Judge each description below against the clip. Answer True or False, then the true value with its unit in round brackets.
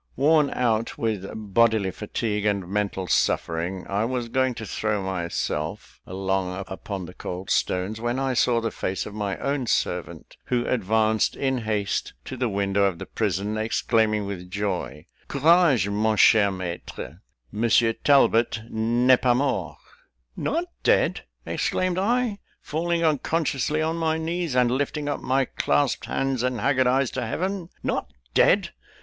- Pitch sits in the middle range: False (115 Hz)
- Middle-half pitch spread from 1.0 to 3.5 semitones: False (5.4 semitones)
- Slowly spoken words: False (150 wpm)